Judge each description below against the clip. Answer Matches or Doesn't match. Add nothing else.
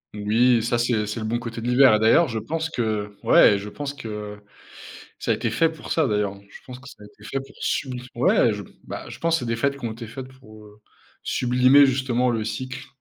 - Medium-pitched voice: Doesn't match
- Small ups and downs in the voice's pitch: Doesn't match